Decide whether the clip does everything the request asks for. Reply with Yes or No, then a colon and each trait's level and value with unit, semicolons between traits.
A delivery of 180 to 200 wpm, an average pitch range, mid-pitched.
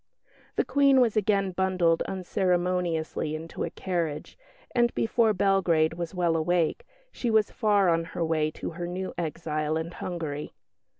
No: average, 145 wpm; average, 3.2 semitones; medium, 175 Hz